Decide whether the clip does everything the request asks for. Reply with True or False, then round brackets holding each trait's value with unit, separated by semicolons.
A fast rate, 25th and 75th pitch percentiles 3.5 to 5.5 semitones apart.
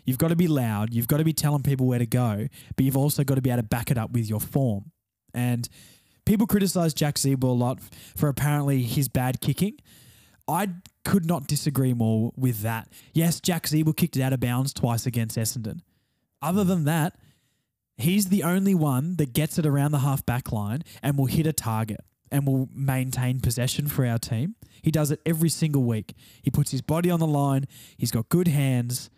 True (210 wpm; 4.2 semitones)